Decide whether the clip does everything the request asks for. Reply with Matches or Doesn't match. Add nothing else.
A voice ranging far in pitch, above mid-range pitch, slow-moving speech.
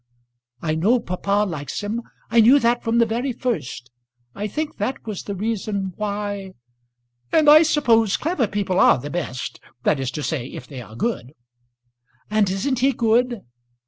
Doesn't match